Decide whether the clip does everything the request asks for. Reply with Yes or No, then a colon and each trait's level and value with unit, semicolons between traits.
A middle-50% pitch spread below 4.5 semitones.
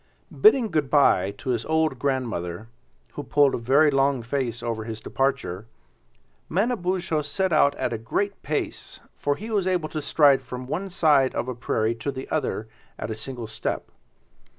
No: average, 5.0 semitones